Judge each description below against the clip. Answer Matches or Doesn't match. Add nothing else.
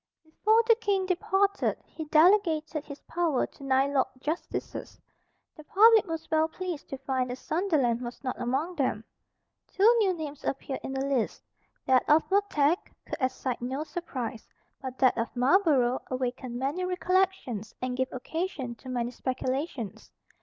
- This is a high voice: Matches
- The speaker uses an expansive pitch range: Matches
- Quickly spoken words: Doesn't match